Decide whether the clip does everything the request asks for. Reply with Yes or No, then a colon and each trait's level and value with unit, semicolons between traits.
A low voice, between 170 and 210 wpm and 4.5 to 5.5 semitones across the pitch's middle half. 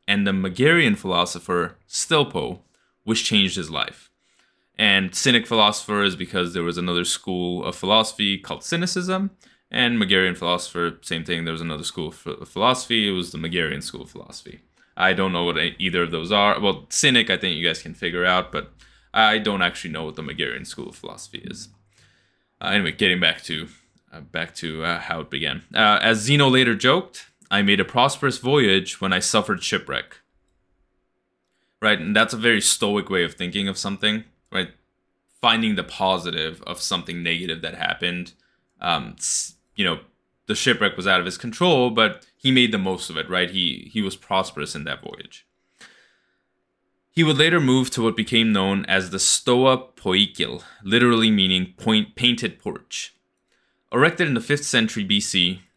Yes: low, 100 Hz; average, 175 wpm; average, 4.9 semitones